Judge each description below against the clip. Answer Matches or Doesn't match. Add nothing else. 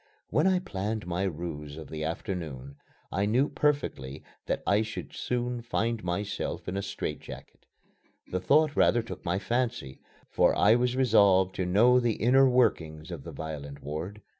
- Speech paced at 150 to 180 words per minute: Matches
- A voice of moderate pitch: Doesn't match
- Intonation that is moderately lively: Doesn't match